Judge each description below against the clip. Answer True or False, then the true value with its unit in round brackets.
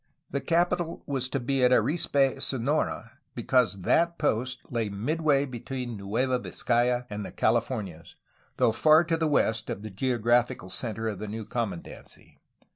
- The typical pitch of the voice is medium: False (125 Hz)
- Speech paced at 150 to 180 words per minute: True (155 wpm)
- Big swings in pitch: False (3.8 semitones)